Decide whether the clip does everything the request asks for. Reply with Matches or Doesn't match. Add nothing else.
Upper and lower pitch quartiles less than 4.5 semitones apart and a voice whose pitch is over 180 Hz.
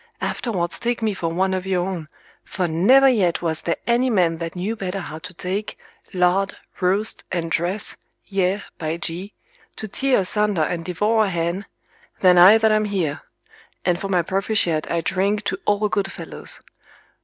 Matches